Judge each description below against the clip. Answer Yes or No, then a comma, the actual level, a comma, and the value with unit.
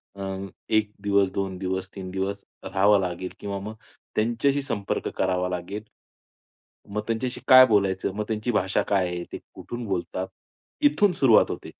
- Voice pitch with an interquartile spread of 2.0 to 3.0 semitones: Yes, average, 2.7 semitones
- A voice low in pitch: Yes, low, 100 Hz